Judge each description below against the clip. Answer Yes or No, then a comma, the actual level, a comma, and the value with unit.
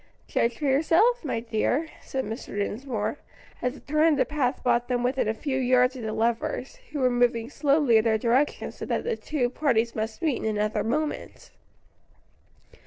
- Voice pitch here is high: Yes, very high, 250 Hz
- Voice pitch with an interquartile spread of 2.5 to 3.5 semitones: No, average, 4.0 semitones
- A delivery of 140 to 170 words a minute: No, average, 185 wpm